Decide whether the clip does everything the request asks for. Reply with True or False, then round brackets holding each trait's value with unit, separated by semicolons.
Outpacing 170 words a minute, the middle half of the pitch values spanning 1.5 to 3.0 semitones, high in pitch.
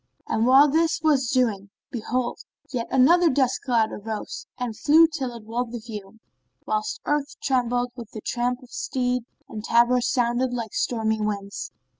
False (165 wpm; 2.7 semitones; 245 Hz)